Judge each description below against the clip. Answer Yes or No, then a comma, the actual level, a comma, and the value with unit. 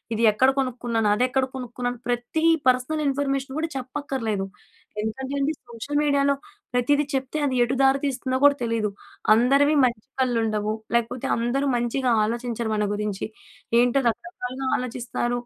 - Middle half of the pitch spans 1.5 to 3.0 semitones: Yes, narrow, 2.6 semitones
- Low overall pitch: No, very high, 250 Hz